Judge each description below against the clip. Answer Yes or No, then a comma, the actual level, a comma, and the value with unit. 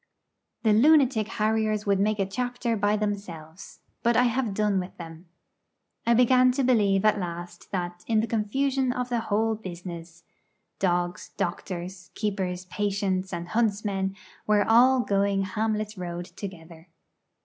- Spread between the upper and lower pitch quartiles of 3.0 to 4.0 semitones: Yes, average, 3.6 semitones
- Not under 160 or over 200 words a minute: No, average, 140 wpm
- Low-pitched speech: No, high, 205 Hz